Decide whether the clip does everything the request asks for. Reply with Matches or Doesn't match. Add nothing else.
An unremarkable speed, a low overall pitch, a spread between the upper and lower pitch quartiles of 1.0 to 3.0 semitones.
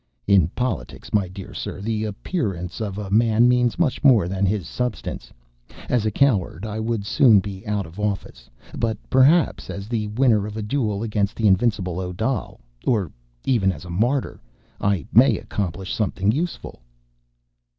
Doesn't match